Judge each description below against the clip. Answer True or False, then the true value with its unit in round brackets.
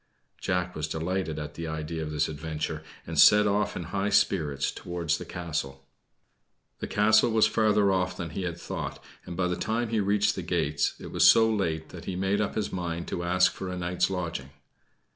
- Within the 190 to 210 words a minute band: True (200 wpm)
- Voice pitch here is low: True (90 Hz)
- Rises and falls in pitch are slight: False (3.8 semitones)